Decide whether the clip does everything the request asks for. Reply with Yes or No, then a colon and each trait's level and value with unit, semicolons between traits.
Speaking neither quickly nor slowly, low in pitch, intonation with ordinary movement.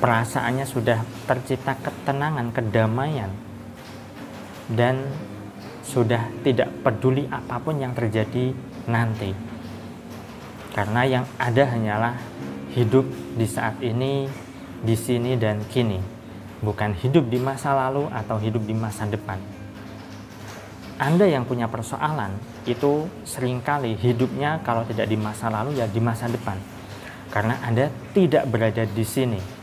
Yes: average, 115 wpm; low, 120 Hz; average, 3.0 semitones